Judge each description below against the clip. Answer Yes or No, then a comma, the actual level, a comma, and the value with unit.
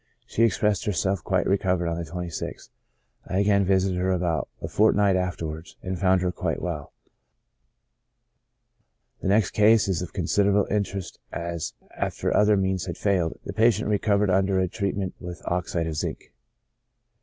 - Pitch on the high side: No, very low, 95 Hz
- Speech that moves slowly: No, average, 155 wpm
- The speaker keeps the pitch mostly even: Yes, narrow, 2.3 semitones